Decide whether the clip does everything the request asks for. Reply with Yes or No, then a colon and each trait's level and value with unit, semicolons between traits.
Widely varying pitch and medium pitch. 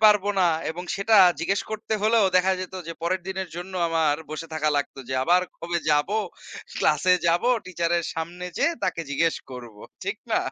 No: narrow, 2.6 semitones; medium, 175 Hz